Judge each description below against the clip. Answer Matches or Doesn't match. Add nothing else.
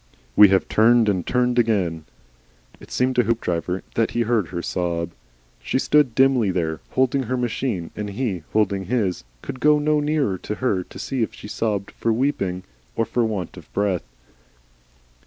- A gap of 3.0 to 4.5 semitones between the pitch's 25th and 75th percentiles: Doesn't match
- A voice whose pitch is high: Doesn't match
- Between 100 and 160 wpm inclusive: Doesn't match